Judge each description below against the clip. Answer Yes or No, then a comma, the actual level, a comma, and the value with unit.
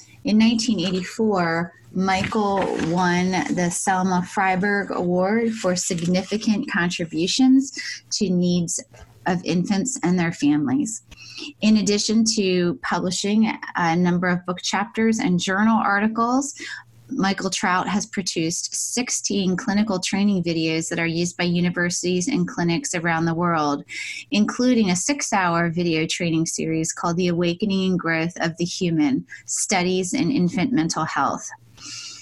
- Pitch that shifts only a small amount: No, average, 3.4 semitones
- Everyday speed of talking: No, slow, 125 wpm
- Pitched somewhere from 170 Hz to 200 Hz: Yes, medium, 185 Hz